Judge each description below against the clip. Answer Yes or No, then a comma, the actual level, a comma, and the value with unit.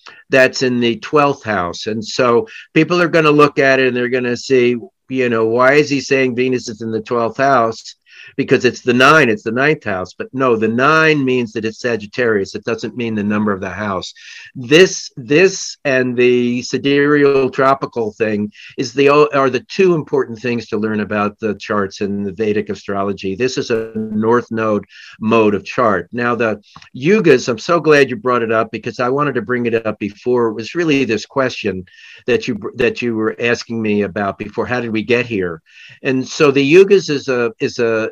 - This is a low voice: Yes, low, 120 Hz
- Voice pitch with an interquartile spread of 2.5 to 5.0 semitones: Yes, average, 3.5 semitones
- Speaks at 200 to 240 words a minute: Yes, fast, 205 wpm